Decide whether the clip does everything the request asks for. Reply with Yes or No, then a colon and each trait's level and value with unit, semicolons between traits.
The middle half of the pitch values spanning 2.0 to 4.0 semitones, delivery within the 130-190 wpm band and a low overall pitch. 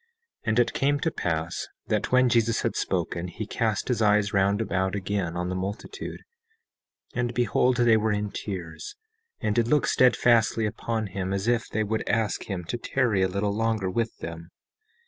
Yes: average, 3.5 semitones; average, 185 wpm; low, 105 Hz